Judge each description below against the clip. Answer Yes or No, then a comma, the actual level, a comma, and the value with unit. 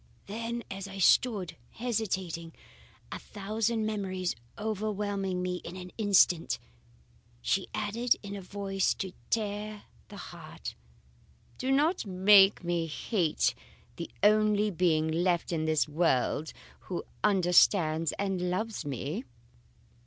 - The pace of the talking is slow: Yes, slow, 115 wpm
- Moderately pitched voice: No, high, 195 Hz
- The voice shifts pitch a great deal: No, average, 3.4 semitones